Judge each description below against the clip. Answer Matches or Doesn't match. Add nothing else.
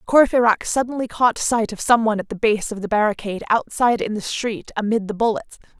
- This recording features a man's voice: Doesn't match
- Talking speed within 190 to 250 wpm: Matches